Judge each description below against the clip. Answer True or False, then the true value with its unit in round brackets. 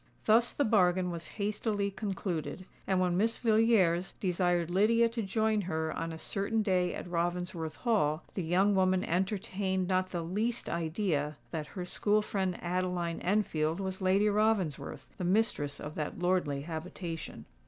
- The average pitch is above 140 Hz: True (185 Hz)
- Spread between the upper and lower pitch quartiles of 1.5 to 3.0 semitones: False (3.4 semitones)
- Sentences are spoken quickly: False (155 wpm)